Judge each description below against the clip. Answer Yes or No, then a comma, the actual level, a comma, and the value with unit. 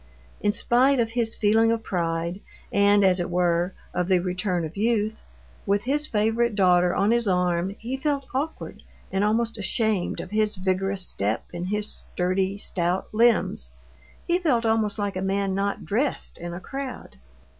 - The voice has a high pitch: Yes, high, 200 Hz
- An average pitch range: Yes, average, 3.8 semitones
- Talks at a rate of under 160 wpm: No, average, 165 wpm